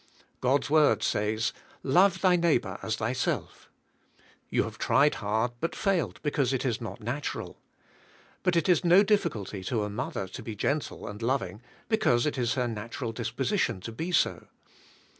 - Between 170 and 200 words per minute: Yes, average, 175 wpm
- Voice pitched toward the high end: No, low, 125 Hz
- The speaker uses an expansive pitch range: Yes, wide, 6.9 semitones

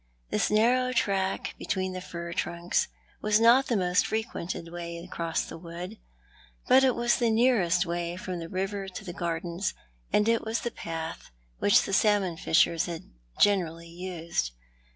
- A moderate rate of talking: Yes, average, 160 wpm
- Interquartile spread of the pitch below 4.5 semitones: Yes, average, 4.0 semitones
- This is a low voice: No, medium, 185 Hz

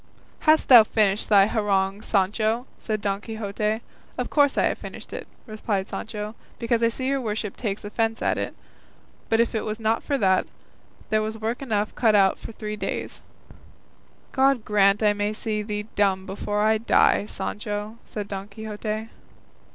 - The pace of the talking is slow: No, average, 170 wpm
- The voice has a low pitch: No, high, 215 Hz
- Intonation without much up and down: Yes, narrow, 1.5 semitones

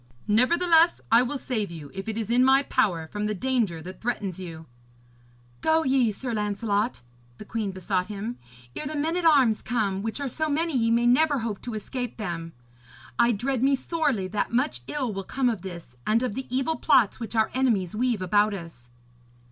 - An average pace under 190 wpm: No, average, 195 wpm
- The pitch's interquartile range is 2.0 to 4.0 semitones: No, average, 4.8 semitones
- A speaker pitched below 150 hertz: No, high, 230 Hz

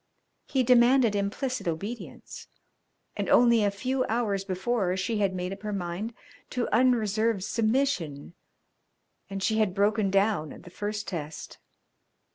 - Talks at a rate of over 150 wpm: No, slow, 135 wpm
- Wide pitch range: No, average, 3.7 semitones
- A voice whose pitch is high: Yes, high, 210 Hz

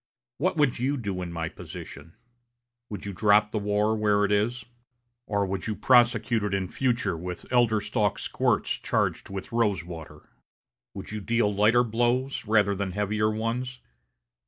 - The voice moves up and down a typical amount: Yes, average, 3.1 semitones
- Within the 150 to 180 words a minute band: Yes, average, 160 wpm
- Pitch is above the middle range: No, low, 105 Hz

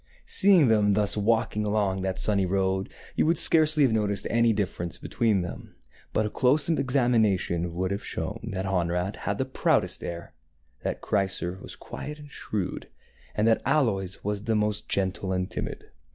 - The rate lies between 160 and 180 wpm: Yes, average, 165 wpm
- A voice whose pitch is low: Yes, low, 105 Hz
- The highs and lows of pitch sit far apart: No, average, 3.5 semitones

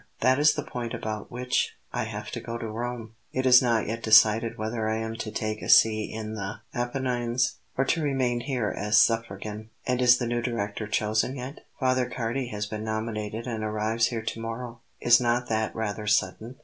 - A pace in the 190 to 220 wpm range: Yes, average, 200 wpm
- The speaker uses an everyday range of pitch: No, narrow, 2.3 semitones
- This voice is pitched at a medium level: No, low, 115 Hz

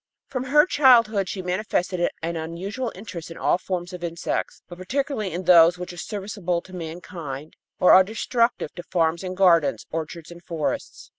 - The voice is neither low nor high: Yes, medium, 180 Hz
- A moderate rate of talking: Yes, average, 170 wpm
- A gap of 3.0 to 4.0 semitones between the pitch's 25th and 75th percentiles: Yes, average, 3.4 semitones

